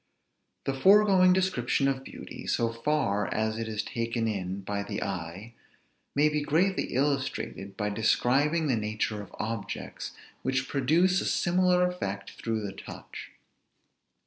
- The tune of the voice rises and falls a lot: Yes, wide, 6.3 semitones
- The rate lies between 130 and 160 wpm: Yes, average, 140 wpm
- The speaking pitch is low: Yes, low, 120 Hz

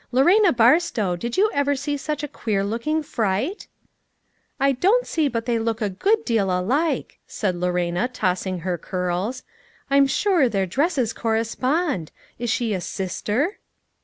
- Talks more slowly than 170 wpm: Yes, average, 160 wpm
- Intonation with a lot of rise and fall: Yes, wide, 7.0 semitones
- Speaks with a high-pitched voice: Yes, high, 235 Hz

